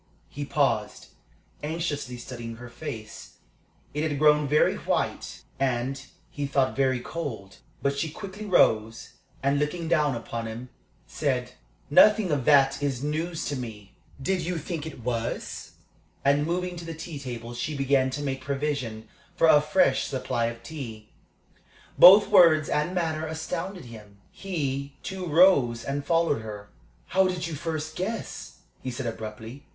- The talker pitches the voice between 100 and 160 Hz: Yes, medium, 140 Hz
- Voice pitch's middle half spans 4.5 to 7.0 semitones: Yes, average, 4.9 semitones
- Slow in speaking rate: No, average, 150 wpm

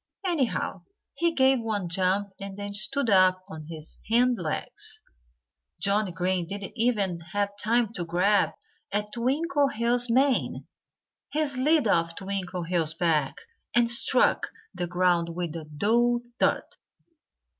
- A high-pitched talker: Yes, high, 200 Hz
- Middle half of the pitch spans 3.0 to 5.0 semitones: No, wide, 5.4 semitones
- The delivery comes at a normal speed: No, slow, 125 wpm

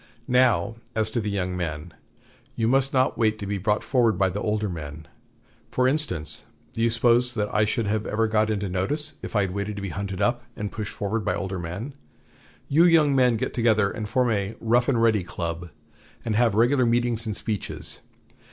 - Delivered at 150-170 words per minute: No, fast, 205 wpm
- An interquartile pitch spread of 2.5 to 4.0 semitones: Yes, average, 3.2 semitones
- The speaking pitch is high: No, low, 110 Hz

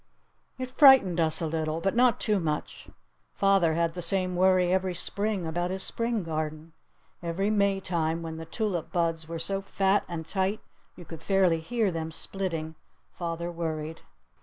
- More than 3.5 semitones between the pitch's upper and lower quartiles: No, average, 3.1 semitones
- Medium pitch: Yes, medium, 175 Hz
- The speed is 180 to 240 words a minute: No, average, 160 wpm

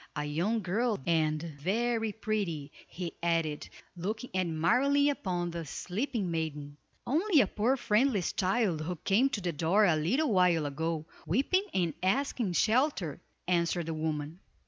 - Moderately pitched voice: Yes, medium, 180 Hz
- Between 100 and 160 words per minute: Yes, average, 145 wpm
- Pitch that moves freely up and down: Yes, wide, 5.9 semitones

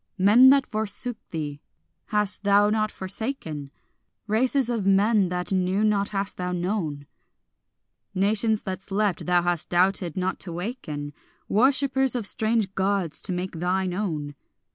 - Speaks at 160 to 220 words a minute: No, average, 140 wpm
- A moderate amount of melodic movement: Yes, average, 3.3 semitones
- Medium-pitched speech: No, high, 195 Hz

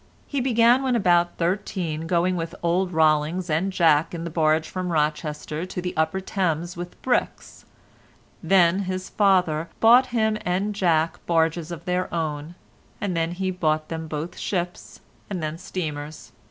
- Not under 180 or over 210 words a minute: No, average, 155 wpm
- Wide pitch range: No, average, 2.8 semitones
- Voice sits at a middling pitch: Yes, medium, 175 Hz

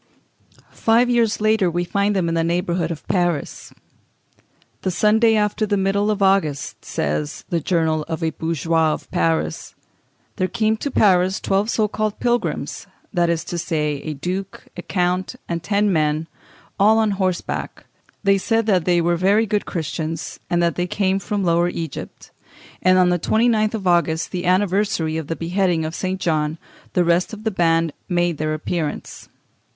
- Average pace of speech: Yes, average, 170 wpm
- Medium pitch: Yes, medium, 180 Hz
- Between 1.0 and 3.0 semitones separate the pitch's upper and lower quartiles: No, average, 3.7 semitones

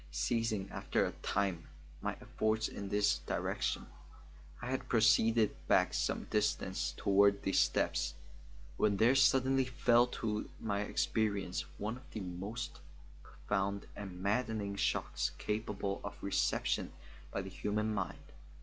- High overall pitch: No, low, 105 Hz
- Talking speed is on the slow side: Yes, slow, 130 wpm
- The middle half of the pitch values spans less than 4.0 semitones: Yes, narrow, 2.5 semitones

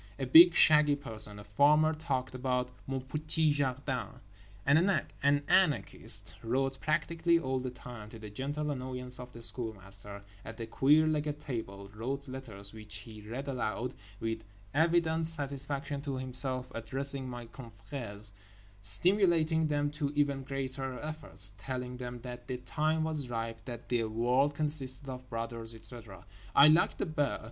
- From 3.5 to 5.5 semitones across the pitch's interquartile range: Yes, average, 4.1 semitones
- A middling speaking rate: Yes, average, 150 wpm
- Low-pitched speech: Yes, low, 130 Hz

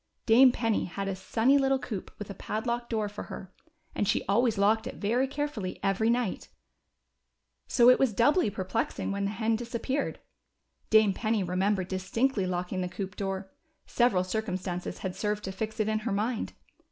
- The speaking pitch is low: No, high, 215 Hz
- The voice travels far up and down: No, average, 3.6 semitones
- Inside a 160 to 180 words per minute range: Yes, average, 175 wpm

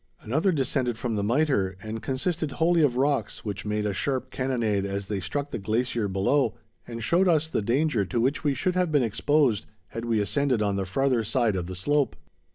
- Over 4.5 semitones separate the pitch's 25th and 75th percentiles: Yes, wide, 5.4 semitones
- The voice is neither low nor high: No, low, 120 Hz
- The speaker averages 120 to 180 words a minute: No, fast, 205 wpm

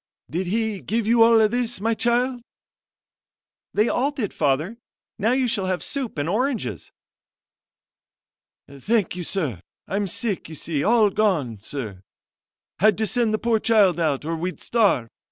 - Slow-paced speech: No, average, 155 wpm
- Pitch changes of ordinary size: No, wide, 5.7 semitones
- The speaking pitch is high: Yes, high, 210 Hz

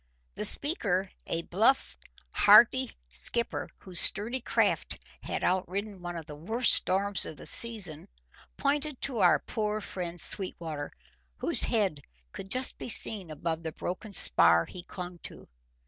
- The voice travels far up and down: No, average, 5.0 semitones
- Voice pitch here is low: No, high, 190 Hz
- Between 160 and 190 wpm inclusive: No, average, 145 wpm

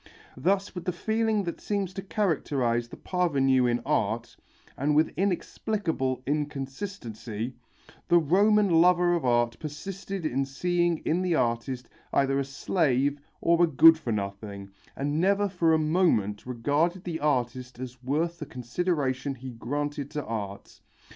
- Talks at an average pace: Yes, average, 145 wpm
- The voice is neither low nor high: Yes, medium, 145 Hz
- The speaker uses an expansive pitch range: Yes, wide, 5.7 semitones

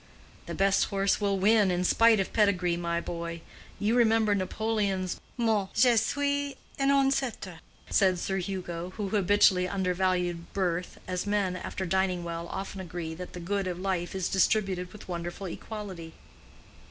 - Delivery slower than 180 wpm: Yes, average, 150 wpm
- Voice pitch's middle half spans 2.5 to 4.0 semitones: Yes, average, 2.8 semitones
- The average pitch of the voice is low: No, high, 190 Hz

